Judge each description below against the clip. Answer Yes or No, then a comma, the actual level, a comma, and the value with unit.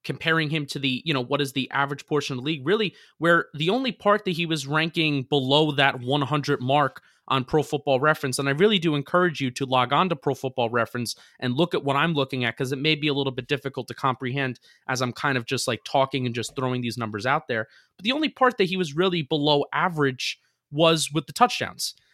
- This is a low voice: No, medium, 145 Hz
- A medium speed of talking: No, fast, 240 wpm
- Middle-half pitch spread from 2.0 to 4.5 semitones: Yes, average, 3.5 semitones